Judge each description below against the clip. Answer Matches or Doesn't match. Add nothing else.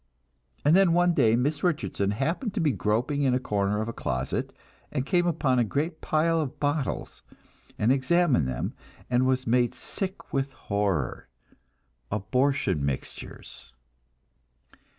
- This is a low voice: Matches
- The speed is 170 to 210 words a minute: Doesn't match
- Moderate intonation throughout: Doesn't match